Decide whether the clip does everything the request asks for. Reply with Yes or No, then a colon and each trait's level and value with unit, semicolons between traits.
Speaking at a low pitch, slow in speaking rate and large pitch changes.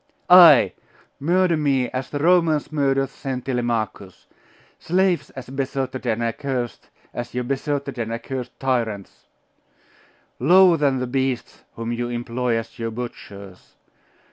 No: low, 130 Hz; slow, 125 wpm; average, 3.2 semitones